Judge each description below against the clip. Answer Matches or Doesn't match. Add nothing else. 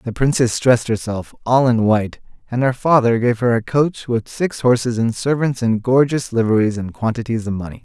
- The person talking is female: Doesn't match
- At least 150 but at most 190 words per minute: Doesn't match